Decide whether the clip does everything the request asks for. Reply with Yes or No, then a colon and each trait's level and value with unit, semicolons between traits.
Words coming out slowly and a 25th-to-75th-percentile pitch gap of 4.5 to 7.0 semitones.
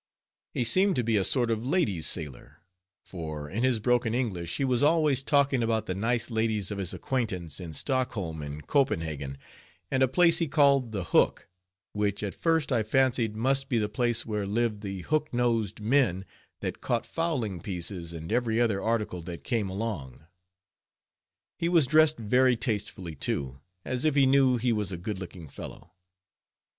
No: average, 175 wpm; wide, 5.6 semitones